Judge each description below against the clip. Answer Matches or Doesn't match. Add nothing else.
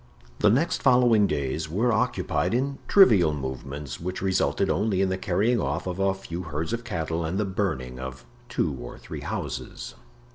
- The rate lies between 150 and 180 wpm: Matches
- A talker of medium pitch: Doesn't match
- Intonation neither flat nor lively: Doesn't match